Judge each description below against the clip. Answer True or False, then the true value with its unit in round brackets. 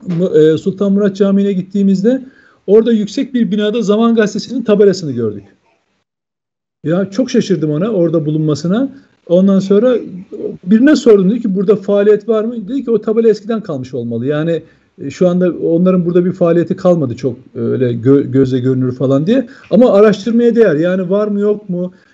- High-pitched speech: True (195 Hz)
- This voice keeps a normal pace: False (165 wpm)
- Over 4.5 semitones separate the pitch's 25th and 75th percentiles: True (5.1 semitones)